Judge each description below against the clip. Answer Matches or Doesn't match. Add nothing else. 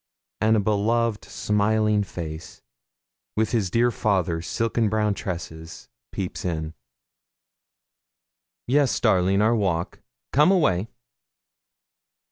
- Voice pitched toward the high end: Doesn't match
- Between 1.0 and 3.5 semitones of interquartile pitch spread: Doesn't match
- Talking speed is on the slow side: Matches